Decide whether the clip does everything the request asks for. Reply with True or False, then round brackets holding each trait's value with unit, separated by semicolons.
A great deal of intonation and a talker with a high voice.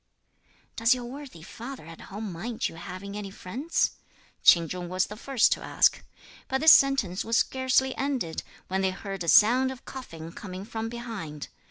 True (6.0 semitones; 215 Hz)